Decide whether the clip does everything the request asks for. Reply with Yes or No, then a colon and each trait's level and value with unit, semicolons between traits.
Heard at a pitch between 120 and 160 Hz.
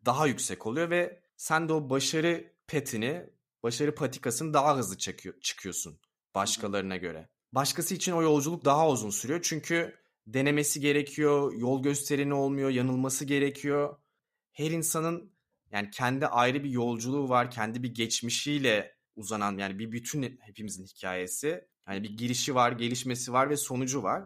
Yes: low, 135 Hz